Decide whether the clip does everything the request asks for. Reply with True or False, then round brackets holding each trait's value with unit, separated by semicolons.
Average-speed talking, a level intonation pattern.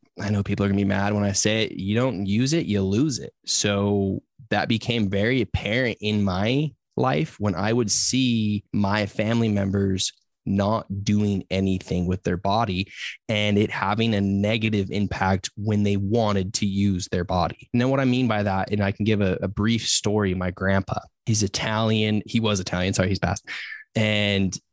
True (190 wpm; 2.1 semitones)